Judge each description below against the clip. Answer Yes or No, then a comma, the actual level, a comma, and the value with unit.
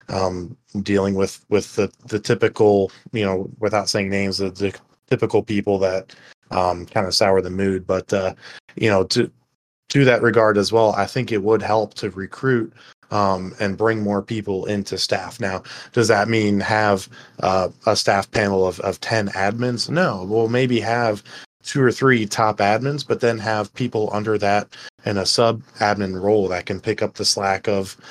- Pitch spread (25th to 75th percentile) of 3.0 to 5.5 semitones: No, narrow, 2.6 semitones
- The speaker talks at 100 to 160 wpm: No, average, 185 wpm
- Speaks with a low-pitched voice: Yes, low, 105 Hz